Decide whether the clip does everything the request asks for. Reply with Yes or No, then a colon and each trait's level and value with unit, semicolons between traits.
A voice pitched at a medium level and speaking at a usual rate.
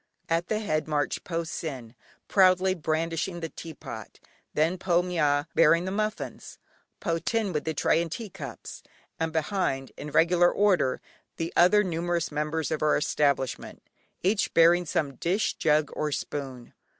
Yes: medium, 165 Hz; average, 150 wpm